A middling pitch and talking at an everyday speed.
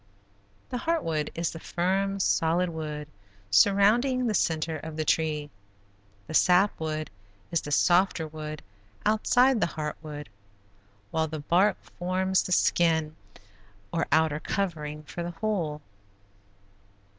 No: medium, 165 Hz; slow, 130 wpm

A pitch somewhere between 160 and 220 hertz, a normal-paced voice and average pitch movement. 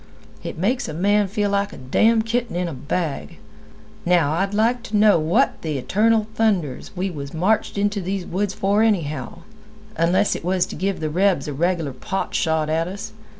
Yes: medium, 185 Hz; average, 190 wpm; average, 4.4 semitones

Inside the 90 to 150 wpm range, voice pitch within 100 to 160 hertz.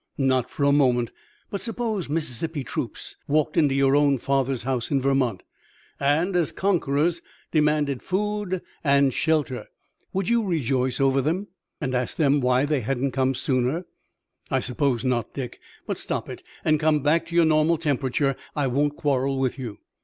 No: average, 165 wpm; medium, 140 Hz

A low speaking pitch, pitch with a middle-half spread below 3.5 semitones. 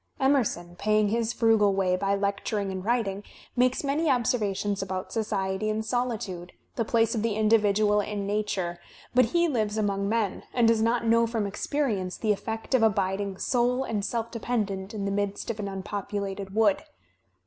No: high, 210 Hz; average, 2.7 semitones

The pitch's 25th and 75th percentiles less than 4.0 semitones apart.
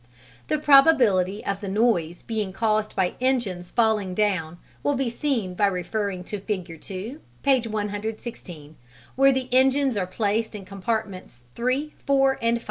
No: average, 5.1 semitones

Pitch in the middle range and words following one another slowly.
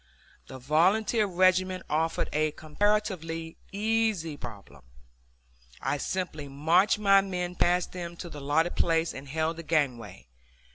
Yes: medium, 165 Hz; slow, 130 wpm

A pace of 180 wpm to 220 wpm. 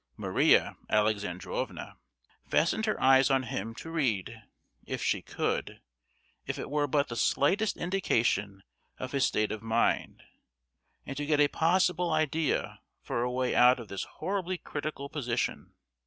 No: average, 140 wpm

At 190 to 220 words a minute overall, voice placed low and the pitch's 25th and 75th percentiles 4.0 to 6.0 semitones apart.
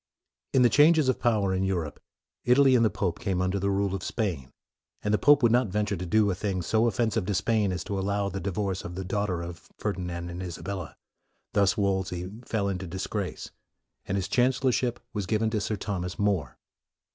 No: fast, 205 wpm; low, 100 Hz; average, 3.0 semitones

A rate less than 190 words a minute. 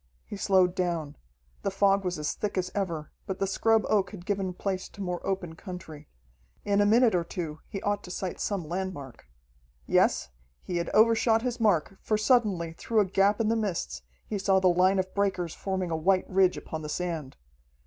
No: average, 200 wpm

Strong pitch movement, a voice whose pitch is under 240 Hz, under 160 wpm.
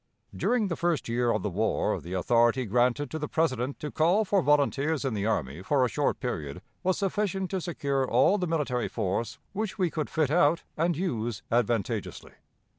No: wide, 6.4 semitones; medium, 140 Hz; average, 190 wpm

